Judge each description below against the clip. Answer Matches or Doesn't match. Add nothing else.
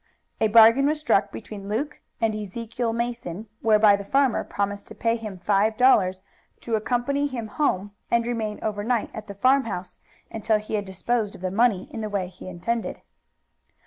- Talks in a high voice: Matches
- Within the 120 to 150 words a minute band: Doesn't match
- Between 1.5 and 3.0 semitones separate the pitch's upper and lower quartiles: Matches